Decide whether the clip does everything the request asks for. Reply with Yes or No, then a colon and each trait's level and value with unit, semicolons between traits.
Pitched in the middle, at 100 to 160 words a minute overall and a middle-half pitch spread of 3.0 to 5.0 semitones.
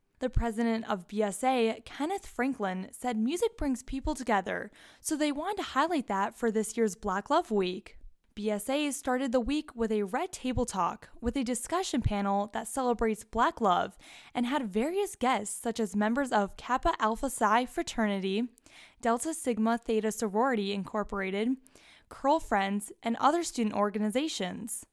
No: high, 235 Hz; average, 150 wpm; average, 4.2 semitones